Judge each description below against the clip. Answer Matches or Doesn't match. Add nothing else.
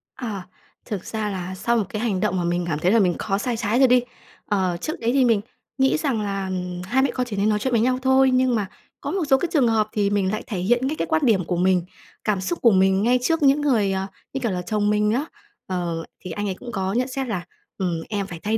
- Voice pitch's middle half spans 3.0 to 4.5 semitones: Doesn't match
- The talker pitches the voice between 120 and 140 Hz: Doesn't match